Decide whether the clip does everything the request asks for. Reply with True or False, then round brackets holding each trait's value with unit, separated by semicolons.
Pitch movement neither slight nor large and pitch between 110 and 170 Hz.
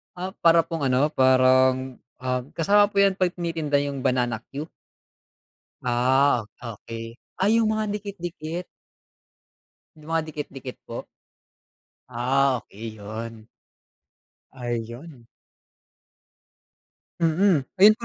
False (5.7 semitones; 140 Hz)